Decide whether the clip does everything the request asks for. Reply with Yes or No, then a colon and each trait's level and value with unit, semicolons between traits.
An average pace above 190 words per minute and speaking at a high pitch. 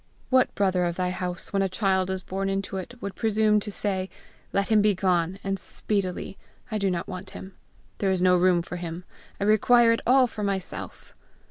Yes: average, 200 wpm; high, 195 Hz